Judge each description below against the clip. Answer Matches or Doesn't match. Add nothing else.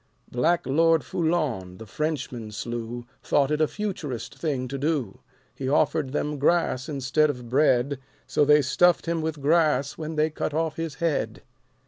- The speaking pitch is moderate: Matches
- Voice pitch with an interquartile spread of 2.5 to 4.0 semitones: Matches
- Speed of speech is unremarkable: Matches